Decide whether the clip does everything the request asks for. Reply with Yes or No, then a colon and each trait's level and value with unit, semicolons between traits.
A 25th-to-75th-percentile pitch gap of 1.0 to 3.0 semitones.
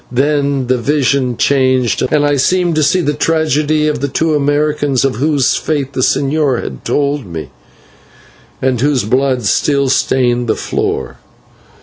Yes: narrow, 2.6 semitones